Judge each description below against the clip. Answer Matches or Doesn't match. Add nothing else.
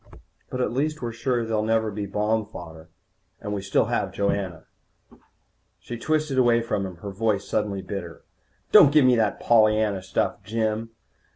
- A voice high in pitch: Doesn't match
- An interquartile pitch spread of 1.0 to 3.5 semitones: Matches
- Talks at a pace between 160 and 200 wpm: Matches